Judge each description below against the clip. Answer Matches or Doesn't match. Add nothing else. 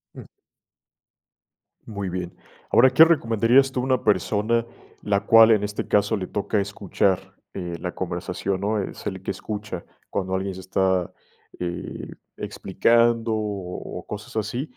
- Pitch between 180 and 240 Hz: Doesn't match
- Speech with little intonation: Doesn't match